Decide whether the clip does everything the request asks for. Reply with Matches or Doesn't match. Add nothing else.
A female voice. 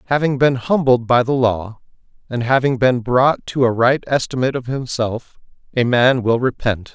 Doesn't match